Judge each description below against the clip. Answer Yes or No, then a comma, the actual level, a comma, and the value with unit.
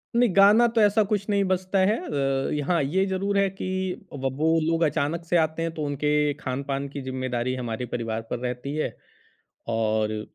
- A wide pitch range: Yes, wide, 6.3 semitones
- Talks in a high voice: No, medium, 150 Hz